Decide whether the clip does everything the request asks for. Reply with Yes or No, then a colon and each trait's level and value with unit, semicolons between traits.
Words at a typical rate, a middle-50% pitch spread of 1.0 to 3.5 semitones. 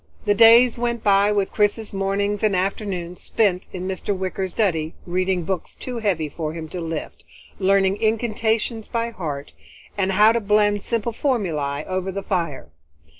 Yes: average, 160 wpm; average, 3.1 semitones